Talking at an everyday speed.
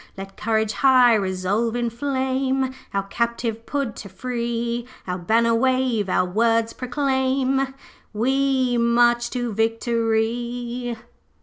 No: slow, 105 wpm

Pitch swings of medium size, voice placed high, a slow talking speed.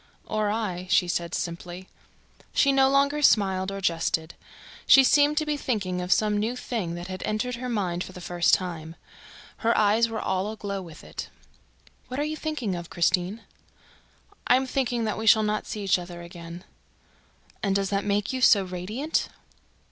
No: average, 4.8 semitones; high, 205 Hz; average, 185 wpm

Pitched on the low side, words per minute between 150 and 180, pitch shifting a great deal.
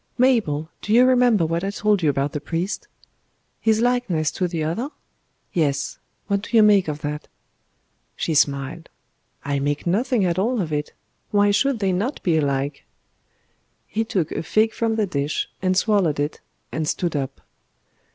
No: medium, 180 Hz; average, 170 wpm; wide, 6.4 semitones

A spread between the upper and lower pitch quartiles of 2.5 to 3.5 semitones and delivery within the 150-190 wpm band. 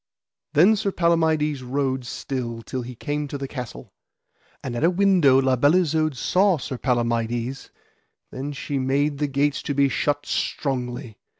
Yes: average, 3.1 semitones; average, 160 wpm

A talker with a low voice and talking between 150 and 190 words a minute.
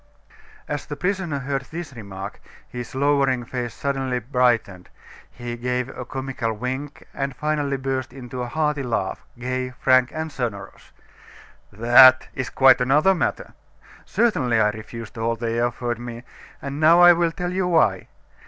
Yes: low, 130 Hz; average, 155 wpm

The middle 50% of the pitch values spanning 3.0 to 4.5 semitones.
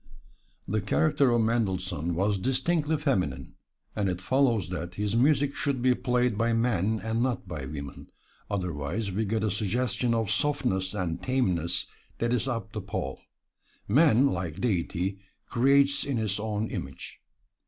No: average, 5.3 semitones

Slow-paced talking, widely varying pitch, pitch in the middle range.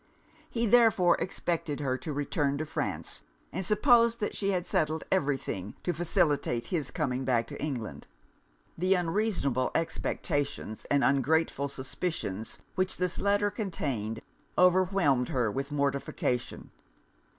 Yes: slow, 130 wpm; wide, 5.7 semitones; medium, 150 Hz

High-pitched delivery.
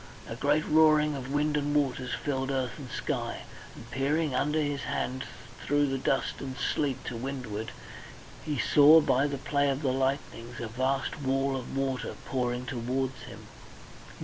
No: low, 135 Hz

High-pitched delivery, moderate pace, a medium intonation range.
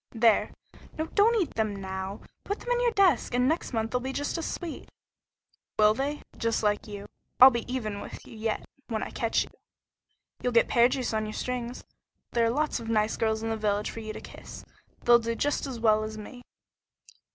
No: high, 230 Hz; fast, 210 wpm; average, 3.5 semitones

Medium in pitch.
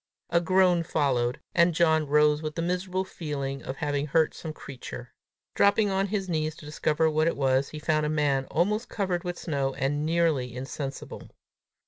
Yes: medium, 155 Hz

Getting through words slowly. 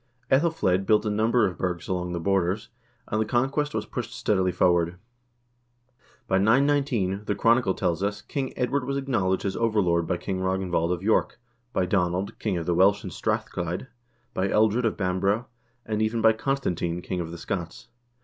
No: average, 180 wpm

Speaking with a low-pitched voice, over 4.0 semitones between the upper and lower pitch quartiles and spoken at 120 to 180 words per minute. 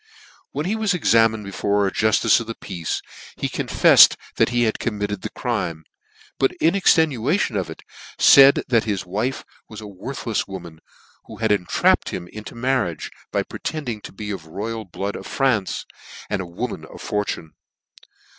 Yes: low, 110 Hz; average, 4.4 semitones; average, 165 wpm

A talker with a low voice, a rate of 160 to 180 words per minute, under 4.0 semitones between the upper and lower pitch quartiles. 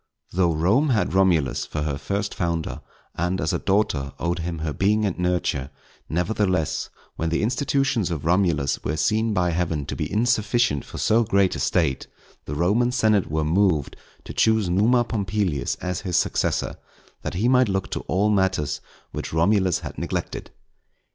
No: very low, 90 Hz; average, 170 wpm; average, 4.7 semitones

